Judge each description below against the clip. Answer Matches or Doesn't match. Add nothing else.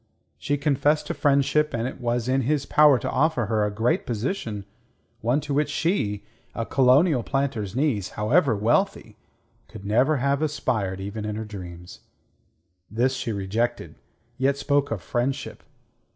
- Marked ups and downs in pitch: Doesn't match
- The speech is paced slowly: Doesn't match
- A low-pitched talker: Matches